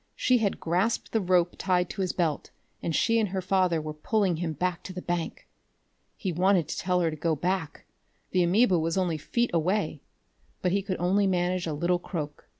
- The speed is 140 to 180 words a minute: No, fast, 205 wpm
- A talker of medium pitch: Yes, medium, 180 Hz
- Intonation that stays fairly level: Yes, narrow, 2.3 semitones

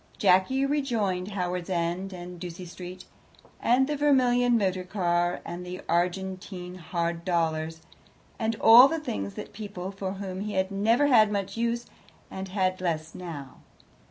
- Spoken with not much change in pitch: No, average, 3.7 semitones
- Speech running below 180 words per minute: Yes, average, 150 wpm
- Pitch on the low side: No, medium, 185 Hz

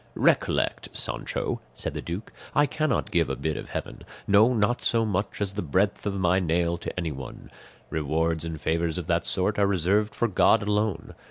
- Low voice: Yes, very low, 95 Hz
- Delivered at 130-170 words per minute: No, average, 185 wpm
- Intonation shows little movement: No, average, 3.9 semitones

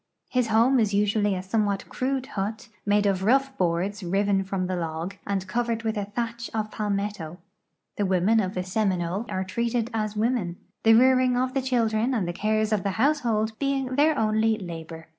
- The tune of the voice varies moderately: Yes, average, 3.5 semitones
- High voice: Yes, high, 215 Hz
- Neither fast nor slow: Yes, average, 190 wpm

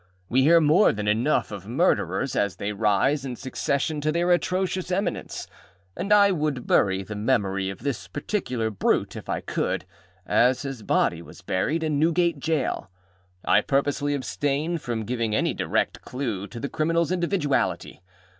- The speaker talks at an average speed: Yes, average, 160 wpm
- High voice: No, medium, 140 Hz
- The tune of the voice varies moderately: No, wide, 6.7 semitones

